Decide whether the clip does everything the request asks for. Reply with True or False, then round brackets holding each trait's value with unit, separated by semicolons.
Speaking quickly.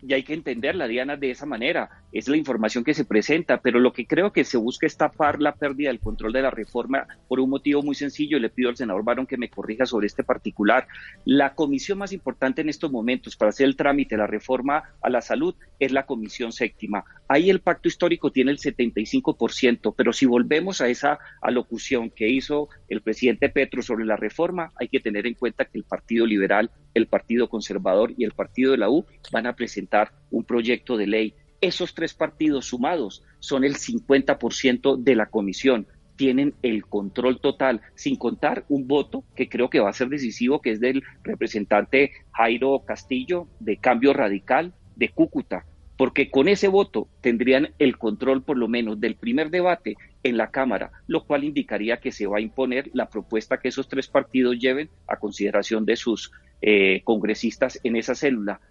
True (195 wpm)